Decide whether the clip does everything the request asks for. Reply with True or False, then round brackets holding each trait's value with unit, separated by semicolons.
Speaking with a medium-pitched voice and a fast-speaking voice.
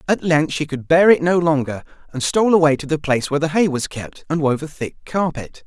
True (155 Hz; 255 wpm)